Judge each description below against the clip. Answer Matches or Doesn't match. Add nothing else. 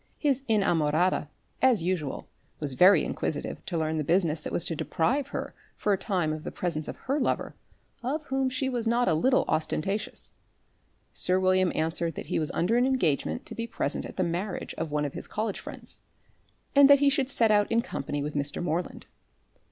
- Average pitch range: Doesn't match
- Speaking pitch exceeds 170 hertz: Matches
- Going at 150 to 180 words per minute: Doesn't match